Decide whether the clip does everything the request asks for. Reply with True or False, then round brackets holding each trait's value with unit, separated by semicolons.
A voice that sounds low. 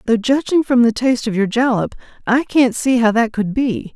False (240 Hz)